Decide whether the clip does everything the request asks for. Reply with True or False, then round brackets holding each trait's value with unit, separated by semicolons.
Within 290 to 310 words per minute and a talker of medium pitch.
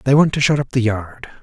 False (295 wpm; 125 Hz)